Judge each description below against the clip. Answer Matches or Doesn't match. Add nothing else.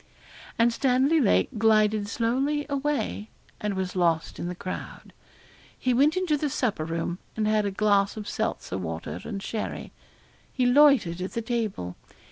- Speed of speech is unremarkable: Matches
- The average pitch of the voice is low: Doesn't match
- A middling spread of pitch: Doesn't match